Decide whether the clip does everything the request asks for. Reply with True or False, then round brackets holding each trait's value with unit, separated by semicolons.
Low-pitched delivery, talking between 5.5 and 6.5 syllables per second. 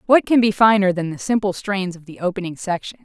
False (195 Hz; 5.9 syllables/s)